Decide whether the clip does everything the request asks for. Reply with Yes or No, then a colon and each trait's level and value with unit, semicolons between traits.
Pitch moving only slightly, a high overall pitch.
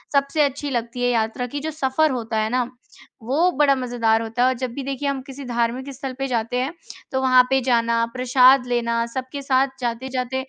Yes: narrow, 2.3 semitones; very high, 255 Hz